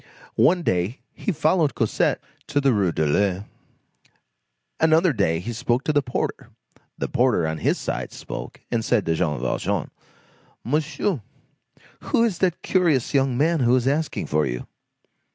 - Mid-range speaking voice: No, low, 125 Hz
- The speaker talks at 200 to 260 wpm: No, average, 155 wpm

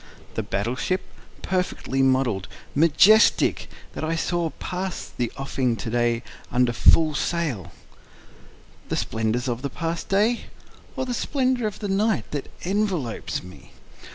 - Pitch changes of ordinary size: No, wide, 8.0 semitones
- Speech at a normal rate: No, slow, 130 wpm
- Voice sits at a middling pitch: Yes, medium, 150 Hz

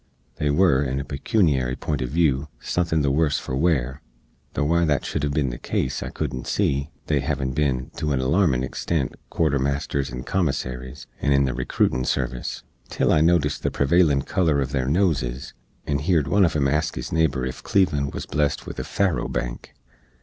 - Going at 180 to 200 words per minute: Yes, average, 195 wpm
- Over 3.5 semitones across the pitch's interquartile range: No, average, 3.2 semitones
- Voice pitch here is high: No, very low, 70 Hz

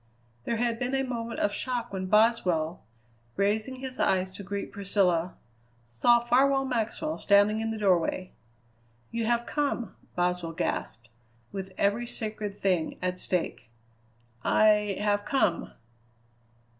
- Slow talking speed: Yes, slow, 130 wpm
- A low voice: No, high, 210 Hz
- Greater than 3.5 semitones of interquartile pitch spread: Yes, average, 4.2 semitones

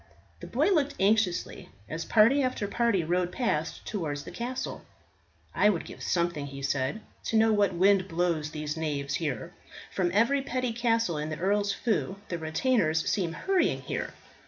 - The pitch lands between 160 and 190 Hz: Yes, medium, 185 Hz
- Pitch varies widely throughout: Yes, wide, 6.2 semitones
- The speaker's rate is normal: Yes, average, 165 wpm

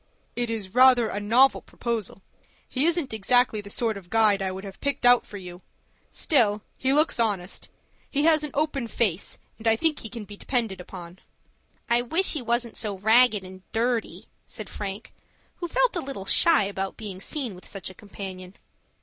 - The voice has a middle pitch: No, high, 225 Hz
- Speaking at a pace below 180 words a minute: No, average, 185 wpm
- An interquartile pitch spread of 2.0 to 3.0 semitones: No, average, 4.4 semitones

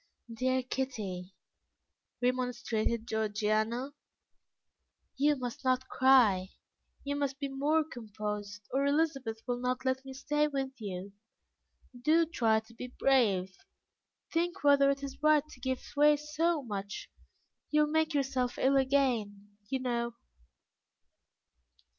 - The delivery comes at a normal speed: No, slow, 125 wpm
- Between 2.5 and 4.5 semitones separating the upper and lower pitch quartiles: Yes, average, 4.2 semitones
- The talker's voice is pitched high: Yes, very high, 260 Hz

